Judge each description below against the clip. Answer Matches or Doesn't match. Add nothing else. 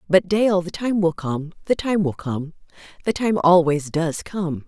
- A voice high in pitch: Doesn't match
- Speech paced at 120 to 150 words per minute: Doesn't match